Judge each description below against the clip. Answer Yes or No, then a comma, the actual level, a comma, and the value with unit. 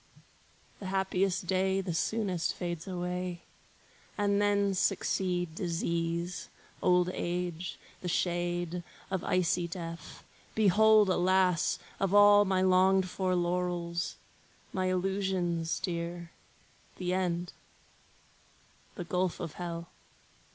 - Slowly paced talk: Yes, slow, 100 wpm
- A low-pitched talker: No, medium, 180 Hz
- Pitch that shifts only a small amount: Yes, narrow, 1.7 semitones